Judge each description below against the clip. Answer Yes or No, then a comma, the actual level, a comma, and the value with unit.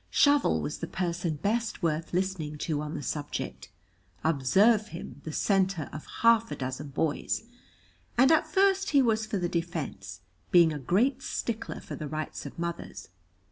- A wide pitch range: Yes, wide, 6.5 semitones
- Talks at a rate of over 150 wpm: Yes, average, 165 wpm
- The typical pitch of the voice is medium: Yes, medium, 170 Hz